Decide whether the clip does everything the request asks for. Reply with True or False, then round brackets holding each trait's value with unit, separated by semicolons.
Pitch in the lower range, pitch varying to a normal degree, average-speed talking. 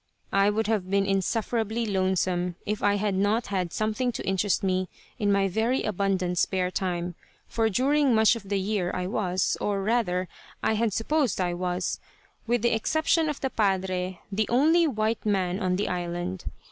False (200 Hz; 3.2 semitones; 175 wpm)